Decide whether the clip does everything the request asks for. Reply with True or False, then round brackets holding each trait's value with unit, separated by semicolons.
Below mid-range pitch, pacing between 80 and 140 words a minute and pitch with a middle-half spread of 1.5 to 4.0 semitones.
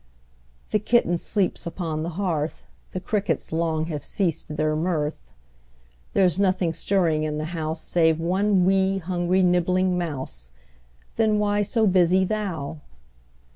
False (175 Hz; 135 wpm; 3.3 semitones)